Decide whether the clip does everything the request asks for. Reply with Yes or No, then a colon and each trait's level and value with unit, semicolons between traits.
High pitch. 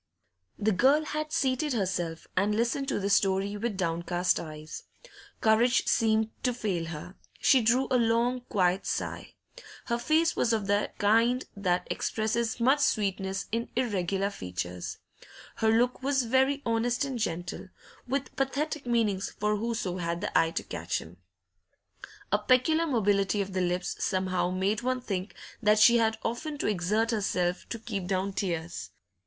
Yes: high, 215 Hz